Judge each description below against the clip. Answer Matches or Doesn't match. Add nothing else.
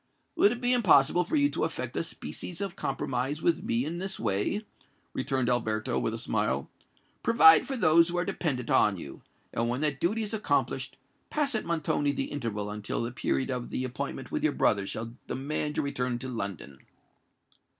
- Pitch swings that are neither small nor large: Doesn't match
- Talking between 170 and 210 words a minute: Matches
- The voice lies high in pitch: Doesn't match